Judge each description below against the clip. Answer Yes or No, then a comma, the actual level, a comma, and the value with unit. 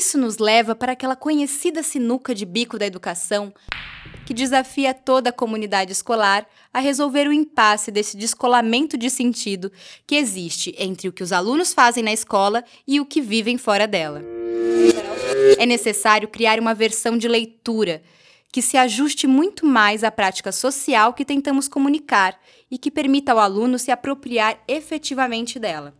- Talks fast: No, average, 155 wpm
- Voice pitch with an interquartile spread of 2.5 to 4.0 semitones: No, average, 4.7 semitones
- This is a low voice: No, high, 235 Hz